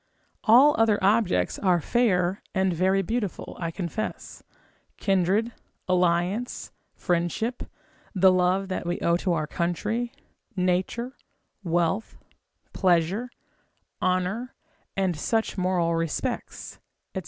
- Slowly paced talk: Yes, slow, 105 wpm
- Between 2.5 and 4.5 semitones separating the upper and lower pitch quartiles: Yes, average, 3.8 semitones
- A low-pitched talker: No, medium, 185 Hz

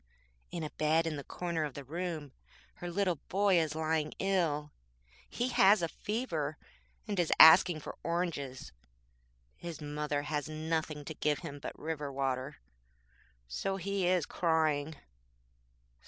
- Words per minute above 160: No, average, 140 wpm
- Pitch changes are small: No, average, 3.0 semitones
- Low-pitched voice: No, medium, 160 Hz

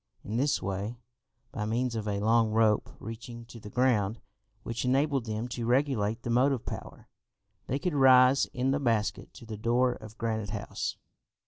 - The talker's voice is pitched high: No, low, 115 Hz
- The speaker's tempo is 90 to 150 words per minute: No, average, 175 wpm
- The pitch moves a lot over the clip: No, average, 2.8 semitones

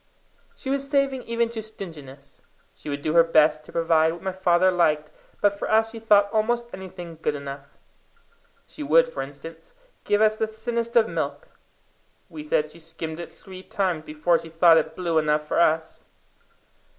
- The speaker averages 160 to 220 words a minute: Yes, average, 180 wpm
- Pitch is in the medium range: Yes, medium, 175 Hz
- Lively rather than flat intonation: Yes, wide, 5.7 semitones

